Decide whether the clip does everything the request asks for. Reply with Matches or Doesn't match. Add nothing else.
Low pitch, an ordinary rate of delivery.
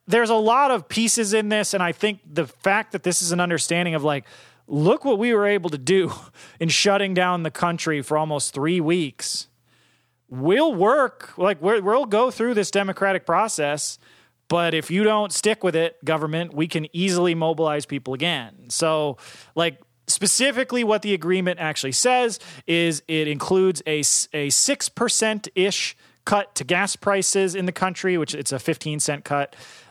Doesn't match